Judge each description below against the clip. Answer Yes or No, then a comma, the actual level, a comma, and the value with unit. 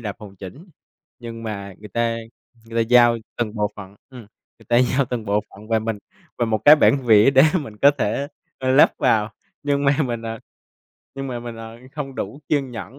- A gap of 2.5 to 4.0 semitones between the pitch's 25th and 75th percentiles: Yes, average, 3.6 semitones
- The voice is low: Yes, low, 115 Hz